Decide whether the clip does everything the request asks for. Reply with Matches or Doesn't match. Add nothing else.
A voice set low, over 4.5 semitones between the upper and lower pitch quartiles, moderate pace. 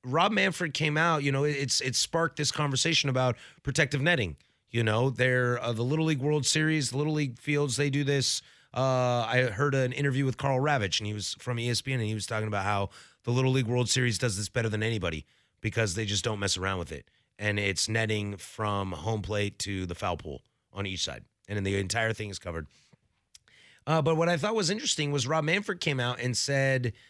Doesn't match